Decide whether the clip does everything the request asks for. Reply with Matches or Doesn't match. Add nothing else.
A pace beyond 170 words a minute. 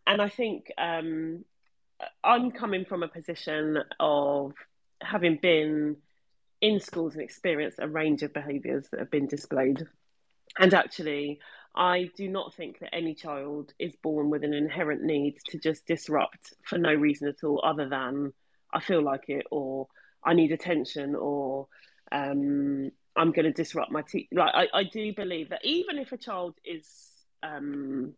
Doesn't match